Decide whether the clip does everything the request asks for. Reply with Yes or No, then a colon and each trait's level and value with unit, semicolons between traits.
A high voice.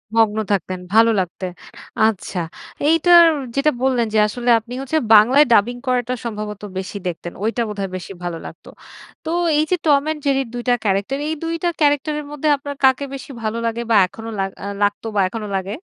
Yes: high, 230 Hz